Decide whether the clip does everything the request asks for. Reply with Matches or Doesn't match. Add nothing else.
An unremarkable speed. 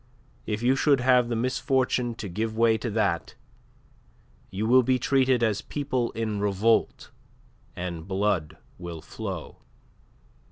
Doesn't match